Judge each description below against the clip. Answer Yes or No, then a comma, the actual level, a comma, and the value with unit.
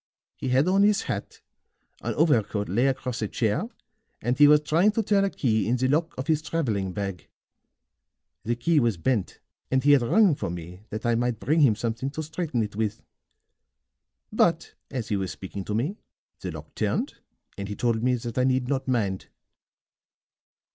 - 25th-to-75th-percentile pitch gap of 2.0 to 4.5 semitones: No, wide, 5.4 semitones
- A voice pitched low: Yes, low, 125 Hz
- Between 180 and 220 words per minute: Yes, average, 190 wpm